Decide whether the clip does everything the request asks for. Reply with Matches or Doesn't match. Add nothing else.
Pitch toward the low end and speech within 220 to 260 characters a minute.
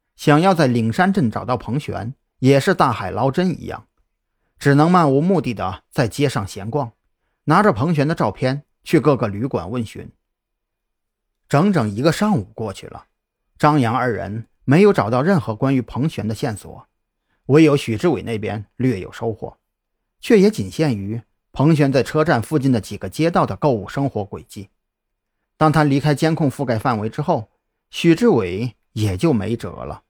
Matches